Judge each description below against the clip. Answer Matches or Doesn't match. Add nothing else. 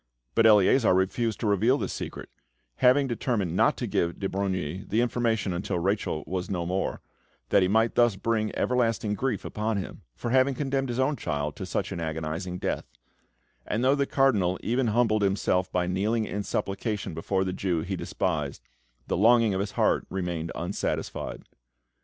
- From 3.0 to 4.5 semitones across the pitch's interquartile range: Matches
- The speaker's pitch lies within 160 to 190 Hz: Doesn't match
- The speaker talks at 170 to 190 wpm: Matches